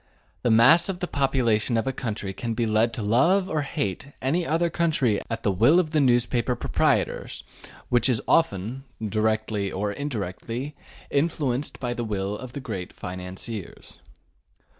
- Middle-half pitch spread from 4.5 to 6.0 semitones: Yes, average, 4.8 semitones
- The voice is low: Yes, low, 120 Hz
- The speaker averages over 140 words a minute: Yes, average, 160 wpm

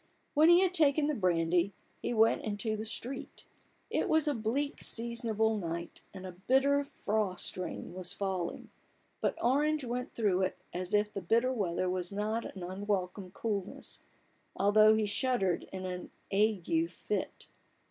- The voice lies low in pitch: No, high, 210 Hz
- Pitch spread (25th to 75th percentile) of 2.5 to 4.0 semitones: No, average, 5.1 semitones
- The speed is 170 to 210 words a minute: No, average, 160 wpm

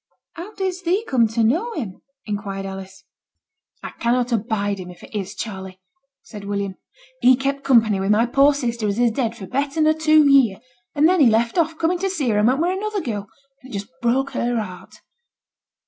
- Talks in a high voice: Yes, high, 240 Hz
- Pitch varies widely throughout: Yes, wide, 6.7 semitones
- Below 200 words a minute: No, fast, 205 wpm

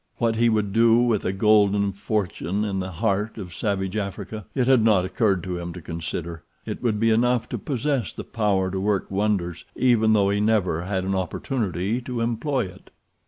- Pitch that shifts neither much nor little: Yes, average, 3.3 semitones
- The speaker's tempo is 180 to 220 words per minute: Yes, average, 190 wpm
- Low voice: Yes, low, 105 Hz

